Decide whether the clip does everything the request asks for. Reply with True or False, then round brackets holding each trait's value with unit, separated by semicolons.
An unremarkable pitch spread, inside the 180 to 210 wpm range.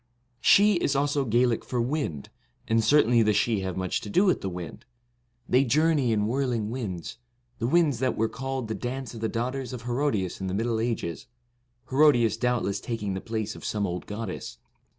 True (4.1 semitones; 195 wpm)